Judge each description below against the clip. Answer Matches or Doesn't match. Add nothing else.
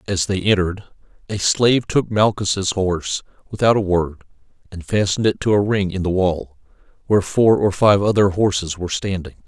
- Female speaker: Doesn't match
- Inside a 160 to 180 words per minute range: Matches